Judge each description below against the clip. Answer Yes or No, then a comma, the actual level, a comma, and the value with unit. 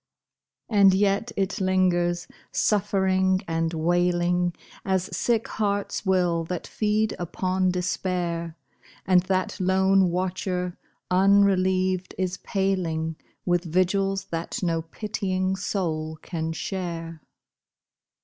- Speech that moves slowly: Yes, slow, 100 wpm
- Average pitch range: No, narrow, 1.7 semitones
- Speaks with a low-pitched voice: No, medium, 185 Hz